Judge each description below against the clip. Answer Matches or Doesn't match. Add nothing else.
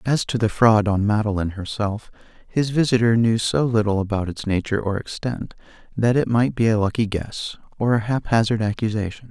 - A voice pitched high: Doesn't match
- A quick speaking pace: Doesn't match